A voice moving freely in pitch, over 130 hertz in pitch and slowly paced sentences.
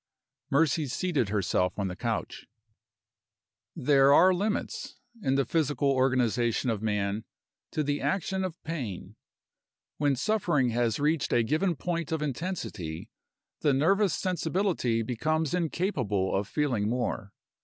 Yes: wide, 6.4 semitones; medium, 140 Hz; slow, 125 wpm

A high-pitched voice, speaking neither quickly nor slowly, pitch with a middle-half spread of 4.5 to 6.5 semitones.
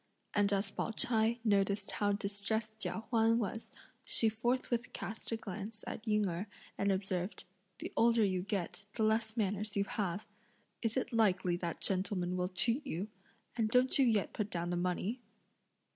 No: high, 210 Hz; average, 170 wpm; average, 2.7 semitones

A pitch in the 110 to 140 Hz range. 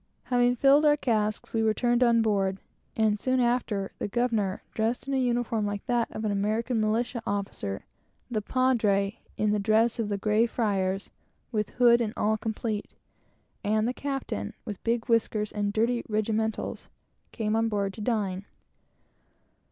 No: high, 220 Hz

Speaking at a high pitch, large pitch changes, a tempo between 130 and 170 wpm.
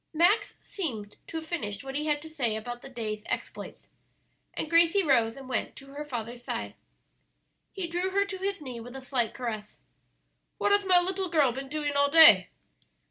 No: very high, 285 Hz; wide, 6.0 semitones; average, 190 wpm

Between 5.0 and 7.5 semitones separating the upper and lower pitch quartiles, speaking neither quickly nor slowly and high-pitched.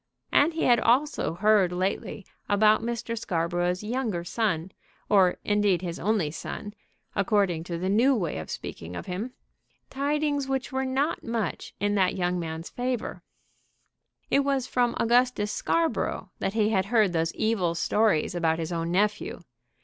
Yes: wide, 5.4 semitones; average, 155 wpm; high, 205 Hz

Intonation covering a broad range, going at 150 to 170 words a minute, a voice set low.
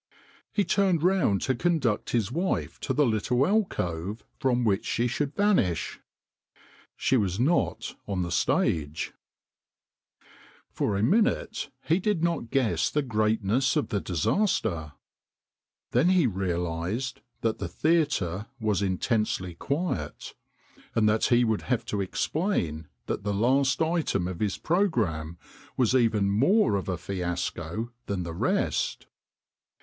No: wide, 7.8 semitones; slow, 135 wpm; low, 110 Hz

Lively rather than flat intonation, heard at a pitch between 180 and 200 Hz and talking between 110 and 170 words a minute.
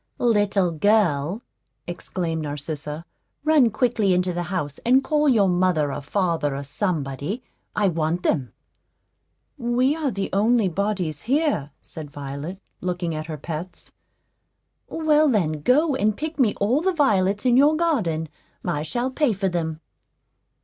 Yes: wide, 7.6 semitones; high, 190 Hz; average, 140 wpm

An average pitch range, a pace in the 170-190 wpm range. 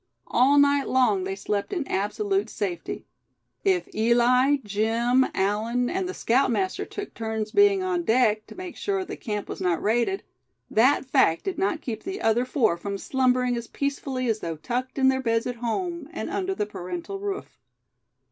No: wide, 6.3 semitones; average, 175 wpm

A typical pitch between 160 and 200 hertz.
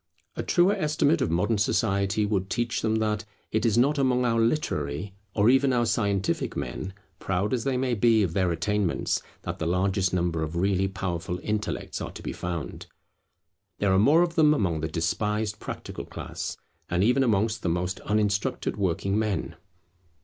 No: low, 105 Hz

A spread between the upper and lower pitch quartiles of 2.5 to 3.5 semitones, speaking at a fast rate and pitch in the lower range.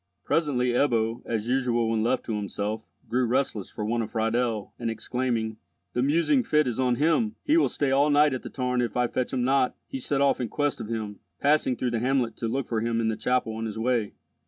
Yes: average, 3.1 semitones; fast, 230 wpm; low, 125 Hz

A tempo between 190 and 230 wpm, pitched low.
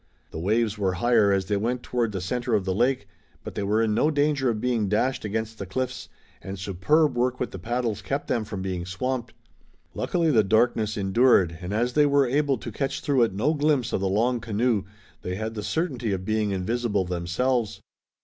Yes: fast, 205 wpm; low, 110 Hz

